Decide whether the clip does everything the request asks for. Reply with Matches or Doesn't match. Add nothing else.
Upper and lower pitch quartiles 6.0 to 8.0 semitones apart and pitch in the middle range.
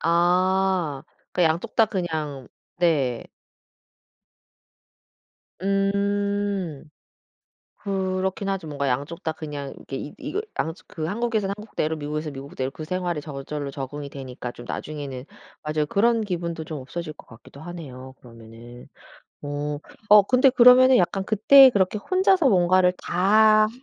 Doesn't match